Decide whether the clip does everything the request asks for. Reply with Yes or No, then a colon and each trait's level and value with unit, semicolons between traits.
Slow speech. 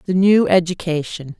Yes: slow, 130 wpm